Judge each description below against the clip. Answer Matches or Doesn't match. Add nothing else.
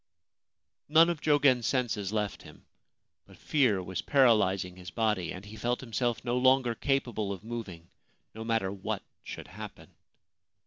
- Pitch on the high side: Doesn't match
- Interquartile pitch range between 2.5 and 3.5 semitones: Doesn't match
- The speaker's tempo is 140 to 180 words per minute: Matches